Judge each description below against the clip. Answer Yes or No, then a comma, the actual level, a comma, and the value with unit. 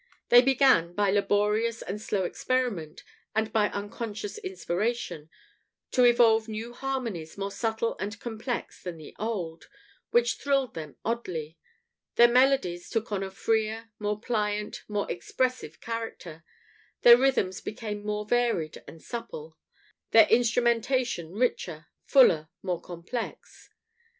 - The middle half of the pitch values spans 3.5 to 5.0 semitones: Yes, average, 4.2 semitones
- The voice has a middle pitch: No, high, 220 Hz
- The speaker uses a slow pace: Yes, slow, 125 wpm